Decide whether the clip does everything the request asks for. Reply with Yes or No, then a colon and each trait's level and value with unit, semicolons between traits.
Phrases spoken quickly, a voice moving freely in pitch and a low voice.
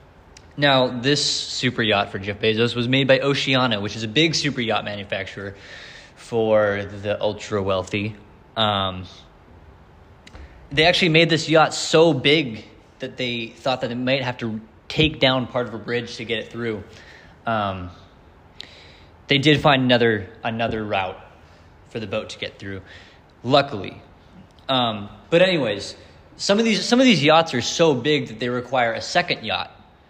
No: average, 160 wpm; wide, 5.7 semitones; low, 115 Hz